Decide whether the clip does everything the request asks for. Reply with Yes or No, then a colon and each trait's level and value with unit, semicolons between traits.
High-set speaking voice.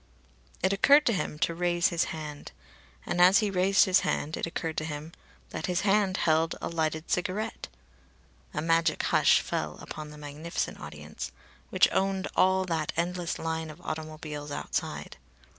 No: medium, 165 Hz